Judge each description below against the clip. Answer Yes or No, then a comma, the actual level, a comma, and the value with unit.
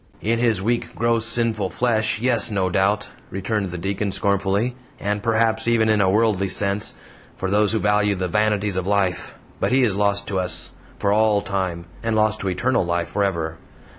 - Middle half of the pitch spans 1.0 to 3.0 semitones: Yes, narrow, 2.5 semitones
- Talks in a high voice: No, low, 105 Hz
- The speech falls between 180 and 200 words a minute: Yes, average, 185 wpm